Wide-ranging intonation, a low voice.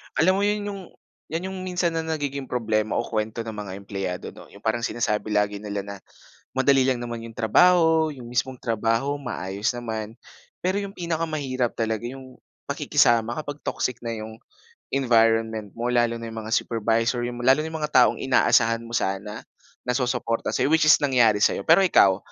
No: average, 4.3 semitones; low, 120 Hz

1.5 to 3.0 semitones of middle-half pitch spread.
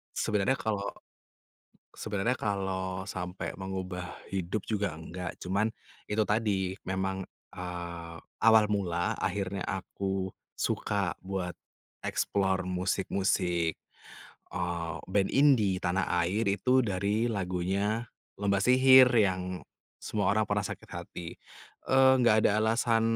Yes: average, 2.7 semitones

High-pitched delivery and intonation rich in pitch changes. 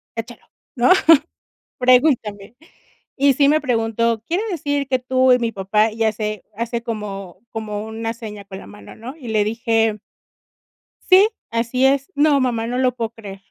No: high, 230 Hz; average, 3.2 semitones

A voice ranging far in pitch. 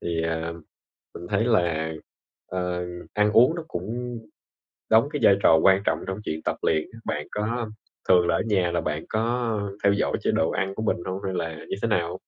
No: average, 4.4 semitones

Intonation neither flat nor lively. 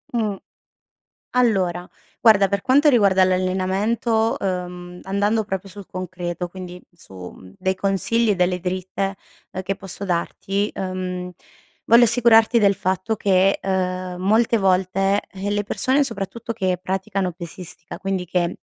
No: narrow, 2.2 semitones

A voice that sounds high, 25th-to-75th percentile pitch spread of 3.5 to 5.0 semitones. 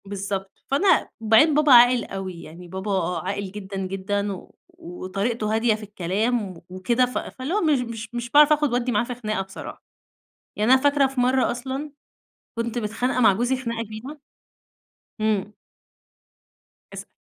Yes: high, 225 Hz; average, 4.2 semitones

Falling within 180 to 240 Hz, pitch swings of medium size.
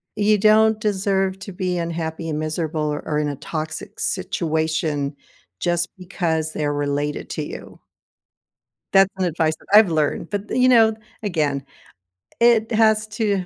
No: medium, 170 Hz; average, 4.6 semitones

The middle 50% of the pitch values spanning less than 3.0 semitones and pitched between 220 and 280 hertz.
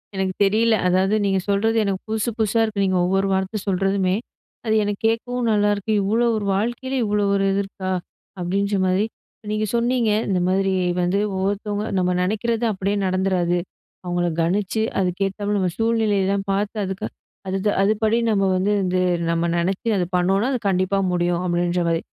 No: narrow, 2.4 semitones; high, 195 Hz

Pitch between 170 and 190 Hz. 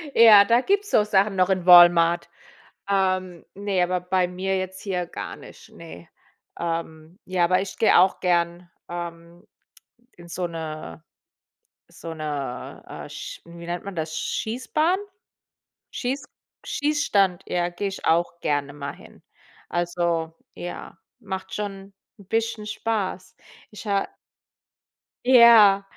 Yes: medium, 185 Hz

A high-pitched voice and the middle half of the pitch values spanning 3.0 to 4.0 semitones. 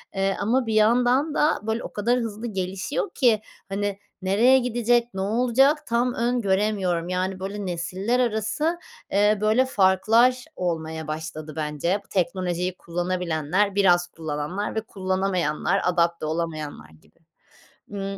No: high, 195 Hz; average, 4.7 semitones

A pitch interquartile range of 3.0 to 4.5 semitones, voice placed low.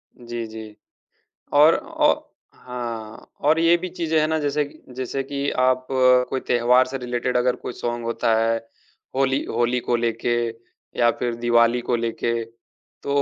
No: narrow, 2.5 semitones; low, 125 Hz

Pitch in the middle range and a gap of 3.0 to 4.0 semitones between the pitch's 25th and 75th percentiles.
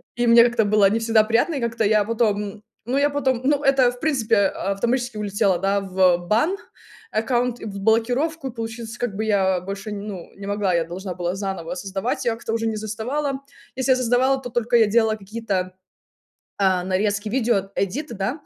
No: high, 220 Hz; average, 3.6 semitones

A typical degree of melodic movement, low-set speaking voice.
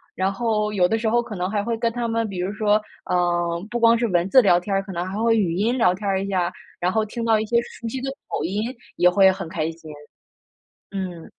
No: average, 4.0 semitones; high, 200 Hz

